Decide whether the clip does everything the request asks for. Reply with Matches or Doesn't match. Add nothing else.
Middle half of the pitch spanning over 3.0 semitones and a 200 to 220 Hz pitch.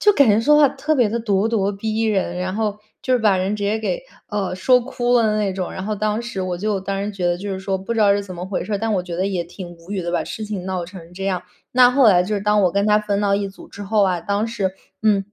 Doesn't match